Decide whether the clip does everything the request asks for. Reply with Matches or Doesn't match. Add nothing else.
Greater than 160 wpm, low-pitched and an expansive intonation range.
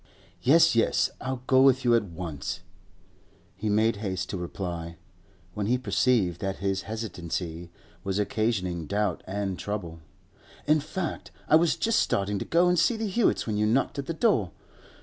Matches